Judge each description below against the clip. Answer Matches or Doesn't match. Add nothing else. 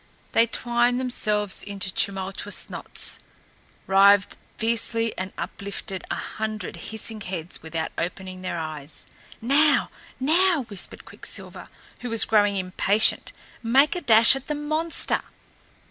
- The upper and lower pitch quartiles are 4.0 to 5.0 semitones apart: Matches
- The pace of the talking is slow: Matches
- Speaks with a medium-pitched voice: Doesn't match